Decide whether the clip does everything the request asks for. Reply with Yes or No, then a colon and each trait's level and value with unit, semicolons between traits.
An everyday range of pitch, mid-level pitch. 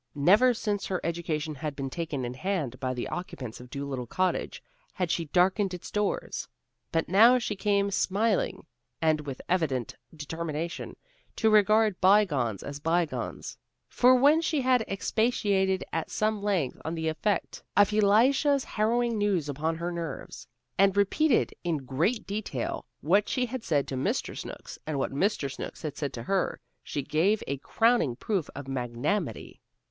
No: wide, 6.4 semitones; medium, 180 Hz